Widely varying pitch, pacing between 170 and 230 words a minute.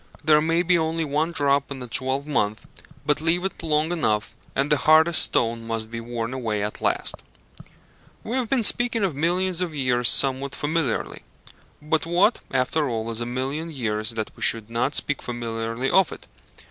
Yes: wide, 5.7 semitones; average, 180 wpm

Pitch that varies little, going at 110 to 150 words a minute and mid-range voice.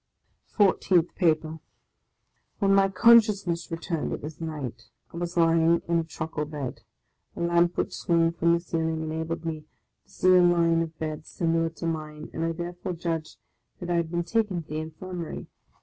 No: narrow, 1.5 semitones; average, 175 wpm; medium, 165 Hz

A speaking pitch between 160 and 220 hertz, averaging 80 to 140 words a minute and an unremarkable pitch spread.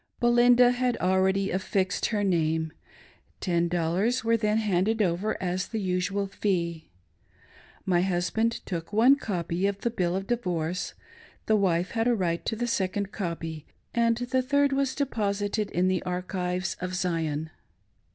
No: high, 190 Hz; average, 150 wpm; average, 4.2 semitones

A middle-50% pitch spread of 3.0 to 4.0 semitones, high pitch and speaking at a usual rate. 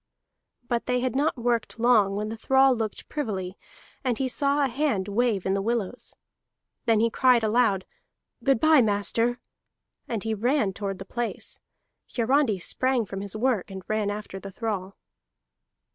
Yes: average, 3.7 semitones; high, 225 Hz; average, 160 wpm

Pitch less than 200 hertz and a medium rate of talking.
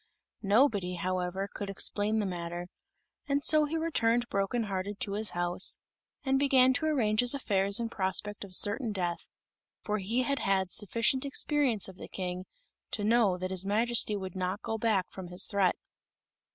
No: high, 205 Hz; average, 170 wpm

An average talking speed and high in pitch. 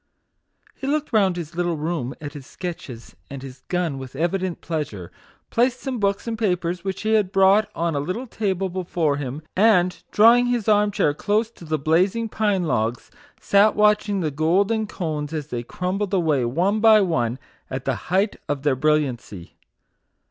No: average, 185 wpm; medium, 180 Hz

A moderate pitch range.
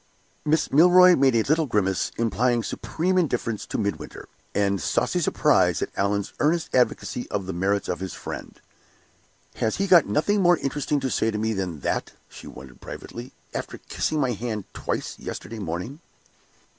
No: wide, 7.1 semitones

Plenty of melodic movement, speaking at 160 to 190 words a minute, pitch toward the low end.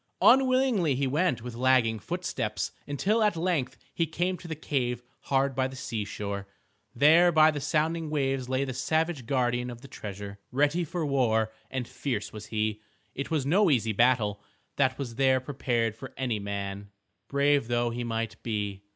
No: average, 4.9 semitones; average, 170 wpm; low, 130 Hz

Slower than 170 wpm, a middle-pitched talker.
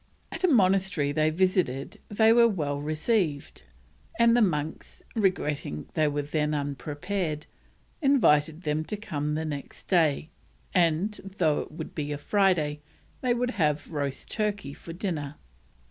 Yes: average, 140 wpm; medium, 160 Hz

